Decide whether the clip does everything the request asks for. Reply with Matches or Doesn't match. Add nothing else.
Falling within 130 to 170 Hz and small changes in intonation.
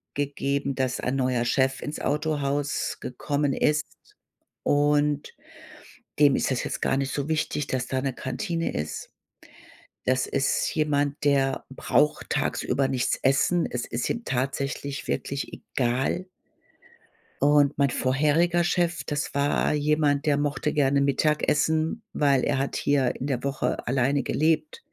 Matches